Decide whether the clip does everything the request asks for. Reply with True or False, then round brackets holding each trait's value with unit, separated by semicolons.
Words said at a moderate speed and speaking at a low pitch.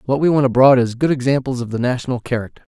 False (240 wpm; 130 Hz)